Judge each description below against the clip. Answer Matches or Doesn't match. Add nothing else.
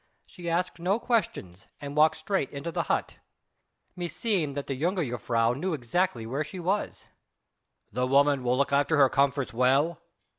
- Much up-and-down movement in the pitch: Doesn't match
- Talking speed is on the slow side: Doesn't match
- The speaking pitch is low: Doesn't match